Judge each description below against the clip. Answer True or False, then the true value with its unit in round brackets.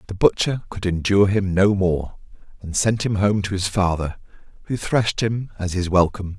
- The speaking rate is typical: True (190 wpm)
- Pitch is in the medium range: False (100 Hz)